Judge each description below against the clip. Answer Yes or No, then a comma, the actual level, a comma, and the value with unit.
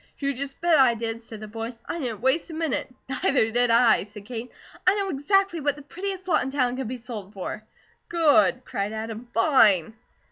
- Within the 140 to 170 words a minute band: No, fast, 205 wpm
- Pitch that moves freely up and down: No, average, 4.9 semitones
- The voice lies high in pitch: Yes, very high, 250 Hz